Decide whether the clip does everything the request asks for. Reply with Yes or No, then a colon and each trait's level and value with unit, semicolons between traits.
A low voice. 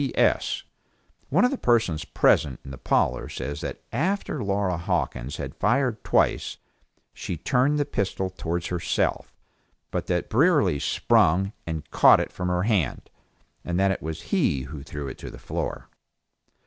Yes: very low, 95 Hz